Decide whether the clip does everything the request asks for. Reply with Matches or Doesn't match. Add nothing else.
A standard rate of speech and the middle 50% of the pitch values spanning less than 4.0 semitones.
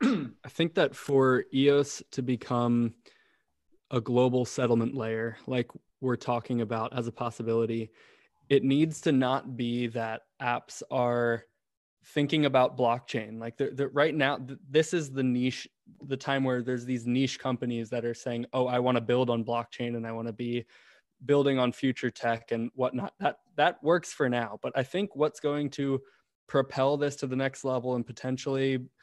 Matches